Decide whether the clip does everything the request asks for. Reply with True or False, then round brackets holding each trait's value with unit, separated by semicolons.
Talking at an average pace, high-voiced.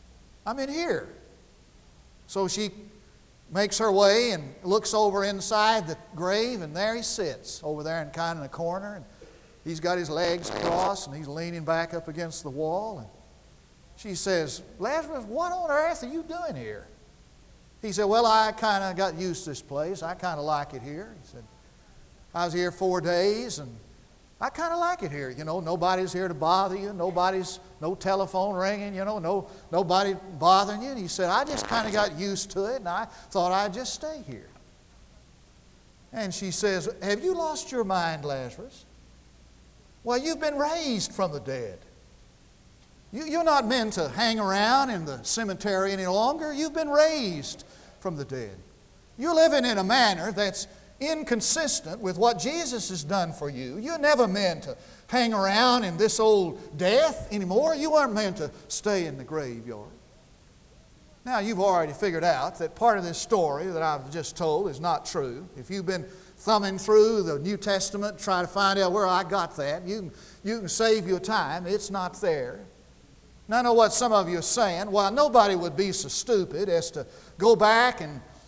True (190 wpm; 195 Hz)